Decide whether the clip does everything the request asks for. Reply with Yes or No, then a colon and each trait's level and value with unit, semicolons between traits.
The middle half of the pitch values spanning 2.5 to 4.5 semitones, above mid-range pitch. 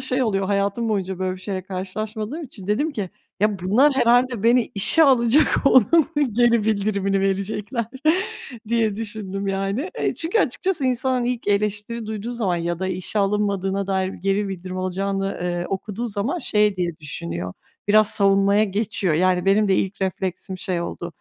Yes: average, 3.5 semitones; high, 200 Hz